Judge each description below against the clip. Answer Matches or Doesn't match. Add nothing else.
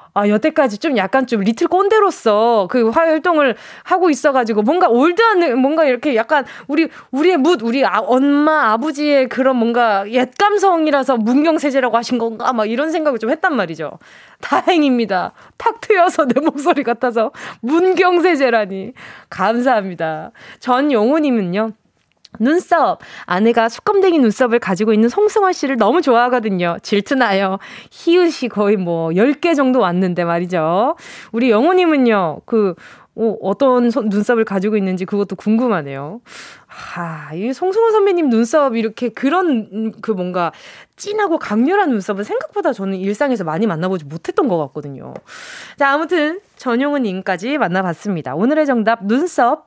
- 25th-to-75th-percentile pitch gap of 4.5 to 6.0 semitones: Doesn't match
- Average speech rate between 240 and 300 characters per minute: Doesn't match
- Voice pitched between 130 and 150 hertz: Doesn't match